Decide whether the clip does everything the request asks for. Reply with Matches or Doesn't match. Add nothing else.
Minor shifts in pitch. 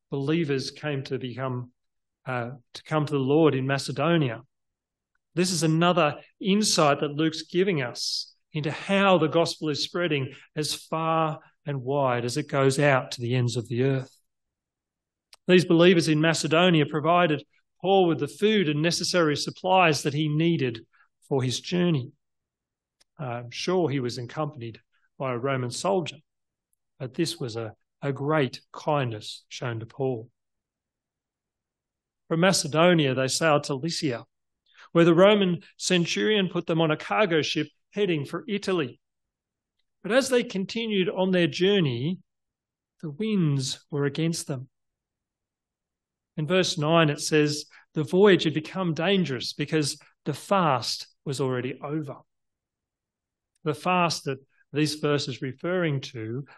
Doesn't match